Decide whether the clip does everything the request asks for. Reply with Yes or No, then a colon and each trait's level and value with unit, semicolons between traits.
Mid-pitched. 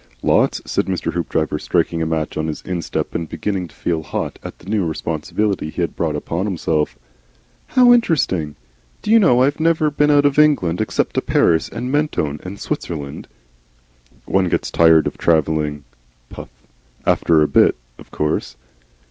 No: very low, 85 Hz